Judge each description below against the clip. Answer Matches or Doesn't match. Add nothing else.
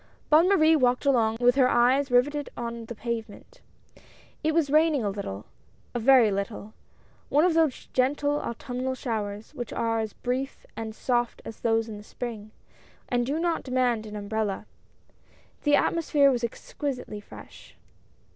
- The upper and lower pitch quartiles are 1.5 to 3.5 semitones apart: Doesn't match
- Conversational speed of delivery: Matches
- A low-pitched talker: Doesn't match